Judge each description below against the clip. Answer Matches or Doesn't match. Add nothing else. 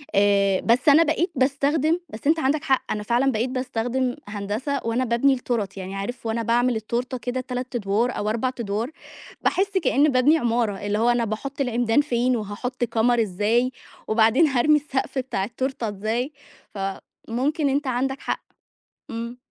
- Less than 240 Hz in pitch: Doesn't match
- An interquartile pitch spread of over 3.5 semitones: Doesn't match